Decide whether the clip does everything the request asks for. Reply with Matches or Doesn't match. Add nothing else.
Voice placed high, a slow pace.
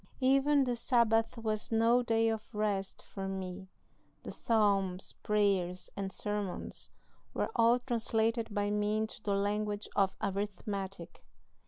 Matches